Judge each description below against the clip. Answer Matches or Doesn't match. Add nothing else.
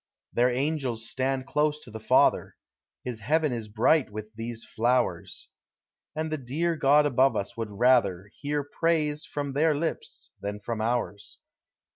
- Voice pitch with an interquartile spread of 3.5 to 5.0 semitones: Matches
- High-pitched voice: Doesn't match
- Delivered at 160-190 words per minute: Doesn't match